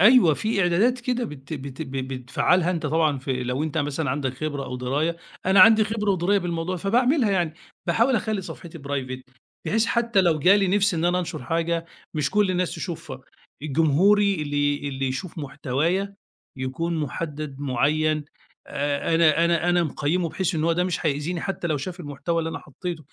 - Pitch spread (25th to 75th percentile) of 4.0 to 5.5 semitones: Yes, average, 4.5 semitones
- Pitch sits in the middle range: Yes, medium, 165 Hz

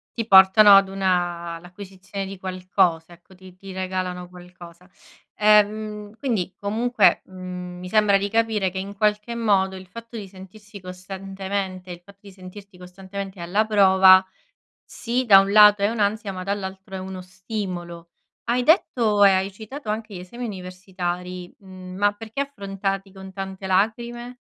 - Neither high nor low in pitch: No, high, 195 Hz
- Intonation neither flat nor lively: No, narrow, 2.3 semitones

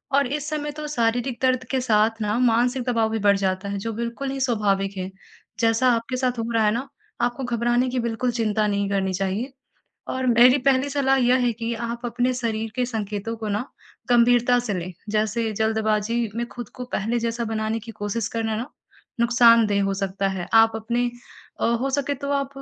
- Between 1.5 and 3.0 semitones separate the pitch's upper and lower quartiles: Yes, narrow, 2.5 semitones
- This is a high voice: Yes, high, 230 Hz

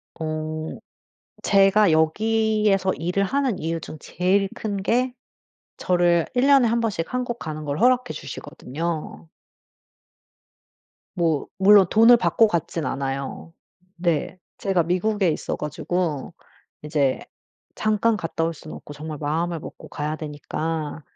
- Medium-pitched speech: Yes, medium, 175 Hz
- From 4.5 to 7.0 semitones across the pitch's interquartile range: Yes, average, 5.2 semitones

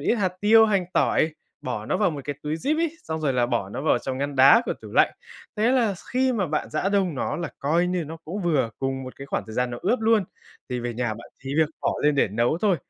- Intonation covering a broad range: Yes, wide, 7.5 semitones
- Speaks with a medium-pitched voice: Yes, medium, 155 Hz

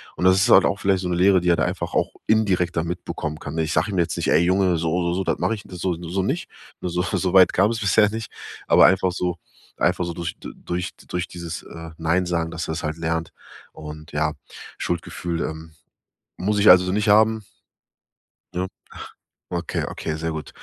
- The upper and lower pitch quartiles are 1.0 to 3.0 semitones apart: Yes, narrow, 2.4 semitones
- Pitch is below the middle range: Yes, very low, 90 Hz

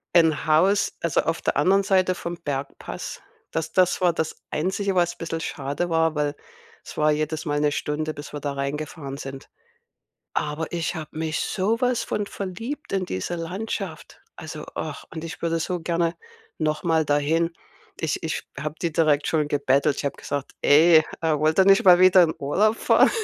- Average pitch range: Yes, average, 3.1 semitones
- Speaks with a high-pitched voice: No, medium, 160 Hz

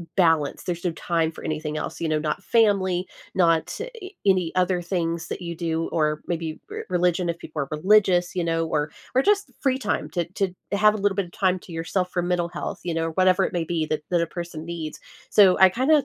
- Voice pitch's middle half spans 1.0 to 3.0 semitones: Yes, narrow, 2.6 semitones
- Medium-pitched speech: Yes, medium, 175 Hz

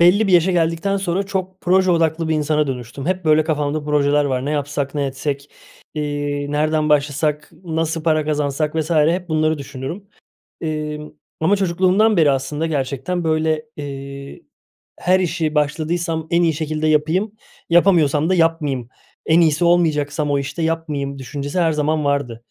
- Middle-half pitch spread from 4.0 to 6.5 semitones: No, average, 2.7 semitones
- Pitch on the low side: No, medium, 155 Hz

